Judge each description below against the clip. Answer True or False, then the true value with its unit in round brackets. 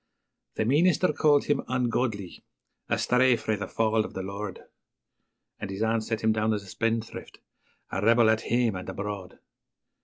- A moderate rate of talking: True (165 wpm)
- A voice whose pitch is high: False (110 Hz)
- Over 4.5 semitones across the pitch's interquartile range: False (2.9 semitones)